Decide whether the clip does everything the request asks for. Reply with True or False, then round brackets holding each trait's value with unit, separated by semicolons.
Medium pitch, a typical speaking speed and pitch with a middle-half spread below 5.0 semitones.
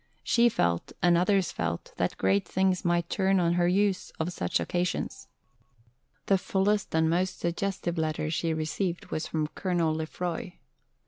True (175 Hz; 155 wpm; 2.9 semitones)